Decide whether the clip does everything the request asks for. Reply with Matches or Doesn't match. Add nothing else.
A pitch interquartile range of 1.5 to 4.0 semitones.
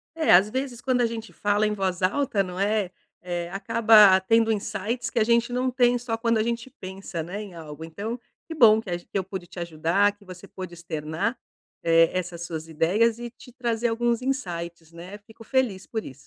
Doesn't match